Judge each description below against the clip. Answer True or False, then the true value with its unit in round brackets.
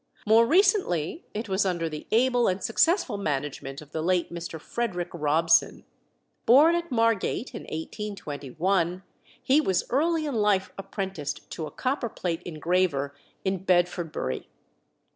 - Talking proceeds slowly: True (130 wpm)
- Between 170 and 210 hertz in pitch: True (190 Hz)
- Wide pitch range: True (6.0 semitones)